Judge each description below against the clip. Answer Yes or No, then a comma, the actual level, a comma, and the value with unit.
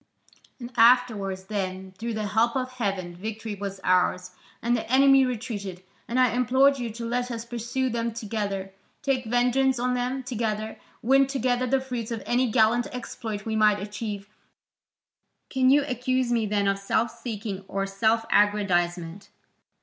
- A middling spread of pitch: Yes, average, 3.5 semitones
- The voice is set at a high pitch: Yes, high, 230 Hz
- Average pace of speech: Yes, average, 155 wpm